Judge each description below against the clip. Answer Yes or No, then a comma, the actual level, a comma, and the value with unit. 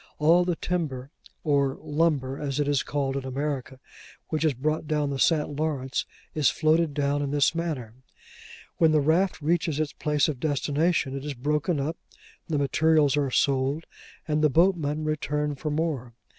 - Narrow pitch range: Yes, narrow, 2.2 semitones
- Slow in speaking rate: No, average, 170 wpm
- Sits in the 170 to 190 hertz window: No, medium, 150 Hz